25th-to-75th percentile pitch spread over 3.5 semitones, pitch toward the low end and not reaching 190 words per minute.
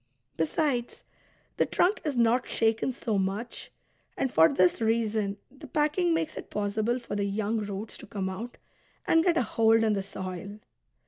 No: average, 4.1 semitones; high, 225 Hz; average, 170 wpm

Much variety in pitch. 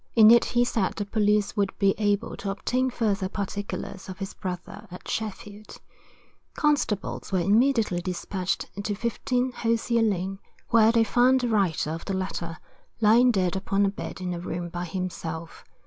No: average, 3.5 semitones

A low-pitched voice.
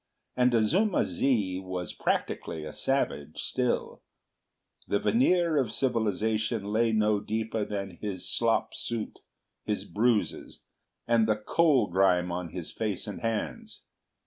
Yes: low, 110 Hz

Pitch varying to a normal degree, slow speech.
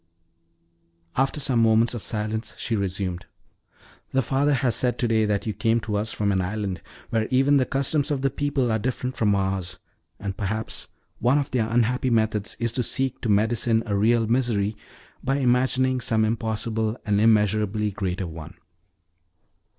No: average, 3.4 semitones; average, 165 wpm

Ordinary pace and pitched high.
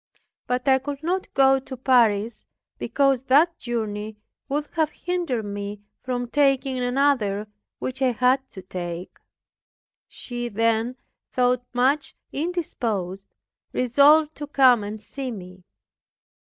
No: slow, 120 wpm; very high, 250 Hz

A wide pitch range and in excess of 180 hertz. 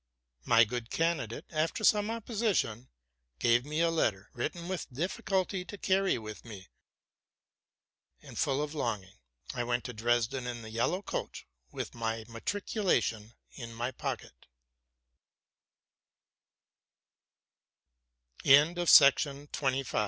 No: wide, 7.6 semitones; low, 125 Hz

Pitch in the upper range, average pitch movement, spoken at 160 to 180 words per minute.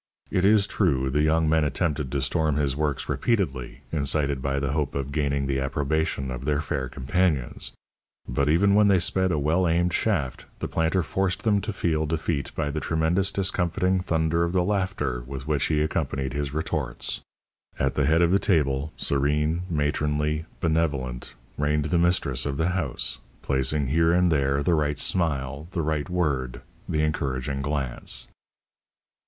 No: very low, 75 Hz; average, 3.5 semitones; average, 170 wpm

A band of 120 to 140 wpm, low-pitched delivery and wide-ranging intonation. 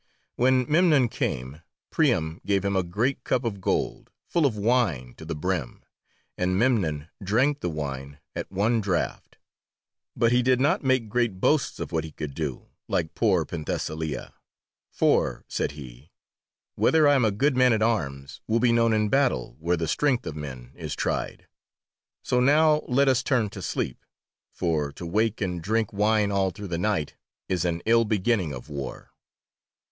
No: average, 170 wpm; low, 100 Hz; wide, 7.5 semitones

